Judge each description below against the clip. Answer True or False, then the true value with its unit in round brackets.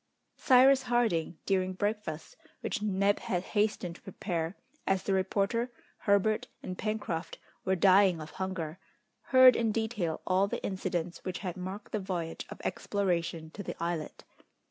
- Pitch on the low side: False (190 Hz)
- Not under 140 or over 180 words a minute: True (145 wpm)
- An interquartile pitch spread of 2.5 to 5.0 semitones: True (3.2 semitones)